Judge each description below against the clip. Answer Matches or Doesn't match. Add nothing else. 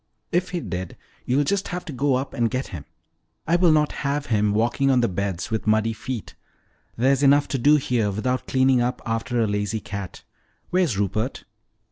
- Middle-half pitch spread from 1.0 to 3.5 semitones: Doesn't match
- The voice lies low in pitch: Matches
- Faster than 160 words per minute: Matches